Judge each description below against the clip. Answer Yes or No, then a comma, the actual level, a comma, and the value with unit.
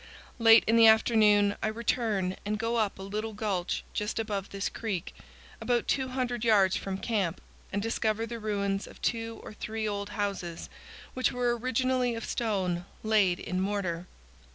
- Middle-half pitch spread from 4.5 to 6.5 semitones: No, narrow, 2.5 semitones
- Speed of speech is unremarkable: Yes, average, 160 wpm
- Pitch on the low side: No, high, 215 Hz